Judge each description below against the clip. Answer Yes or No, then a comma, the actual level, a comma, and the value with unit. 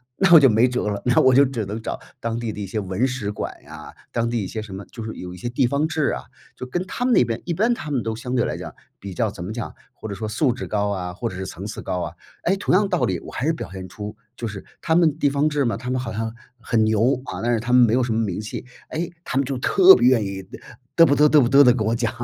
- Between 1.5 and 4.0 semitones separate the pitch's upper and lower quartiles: No, average, 4.8 semitones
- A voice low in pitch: Yes, low, 120 Hz